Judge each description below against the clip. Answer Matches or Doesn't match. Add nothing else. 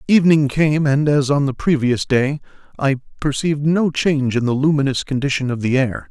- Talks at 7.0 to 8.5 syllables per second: Doesn't match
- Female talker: Doesn't match